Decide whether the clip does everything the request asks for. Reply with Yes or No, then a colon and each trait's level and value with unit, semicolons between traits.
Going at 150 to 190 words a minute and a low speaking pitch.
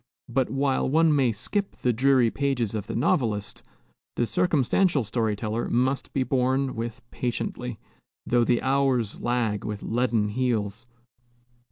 No: average, 140 wpm; low, 125 Hz